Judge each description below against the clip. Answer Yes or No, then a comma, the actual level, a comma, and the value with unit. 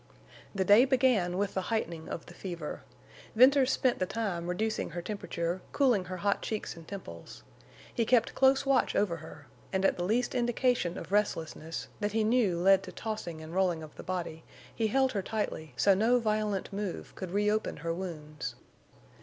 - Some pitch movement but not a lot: Yes, average, 4.4 semitones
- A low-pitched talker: No, high, 195 Hz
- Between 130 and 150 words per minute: No, average, 180 wpm